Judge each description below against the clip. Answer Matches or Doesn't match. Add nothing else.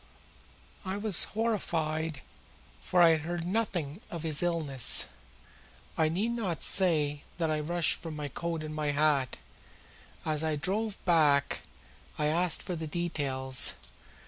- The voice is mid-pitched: Matches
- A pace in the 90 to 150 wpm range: Matches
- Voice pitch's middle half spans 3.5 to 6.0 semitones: Doesn't match